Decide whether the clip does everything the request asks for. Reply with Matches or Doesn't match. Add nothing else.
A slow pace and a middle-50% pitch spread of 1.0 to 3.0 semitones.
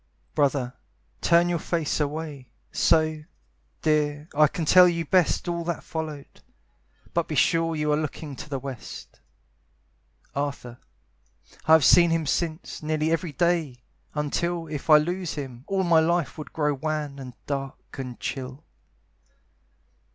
Doesn't match